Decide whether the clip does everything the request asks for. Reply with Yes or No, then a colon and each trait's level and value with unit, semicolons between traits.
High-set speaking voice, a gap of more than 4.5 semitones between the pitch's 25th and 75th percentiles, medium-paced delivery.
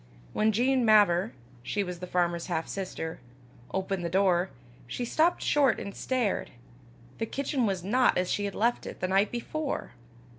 Yes: high, 200 Hz; average, 5.1 semitones; average, 170 wpm